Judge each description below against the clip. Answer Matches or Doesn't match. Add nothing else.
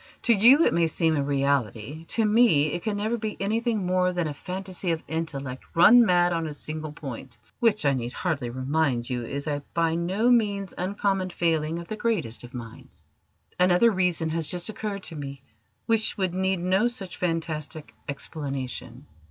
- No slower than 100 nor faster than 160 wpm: Doesn't match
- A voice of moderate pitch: Matches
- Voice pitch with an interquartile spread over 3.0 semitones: Matches